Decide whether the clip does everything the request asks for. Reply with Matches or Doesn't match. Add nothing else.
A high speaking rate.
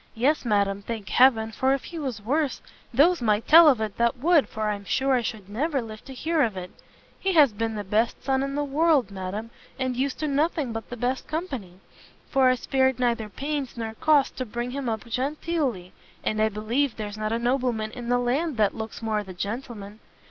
Matches